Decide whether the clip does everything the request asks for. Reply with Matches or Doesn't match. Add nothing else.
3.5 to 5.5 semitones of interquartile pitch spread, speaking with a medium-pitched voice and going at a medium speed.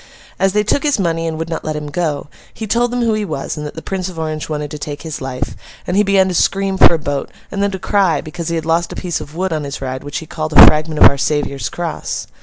Doesn't match